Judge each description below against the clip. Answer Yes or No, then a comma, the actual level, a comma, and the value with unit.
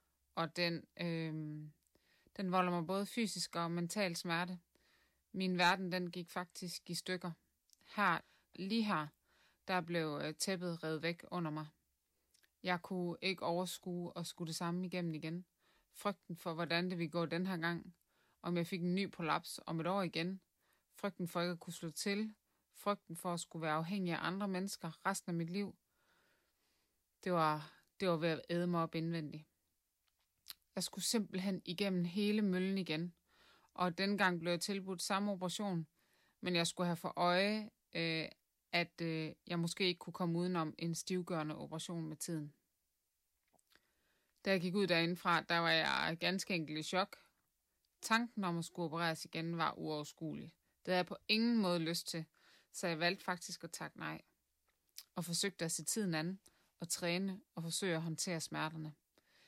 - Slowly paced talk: No, average, 170 wpm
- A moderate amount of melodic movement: No, narrow, 2.1 semitones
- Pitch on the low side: No, medium, 175 Hz